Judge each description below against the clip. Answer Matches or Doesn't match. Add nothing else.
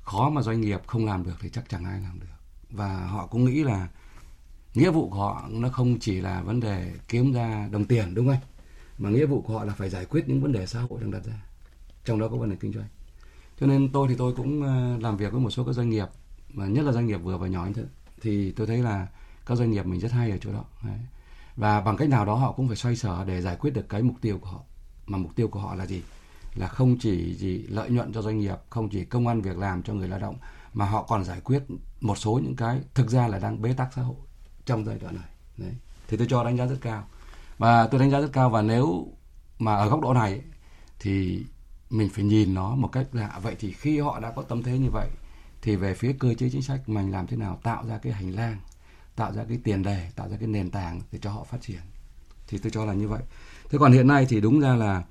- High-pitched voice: Doesn't match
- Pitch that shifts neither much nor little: Matches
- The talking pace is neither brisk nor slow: Doesn't match